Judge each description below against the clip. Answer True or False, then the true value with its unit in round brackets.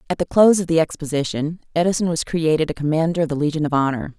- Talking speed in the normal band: False (230 wpm)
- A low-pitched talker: False (160 Hz)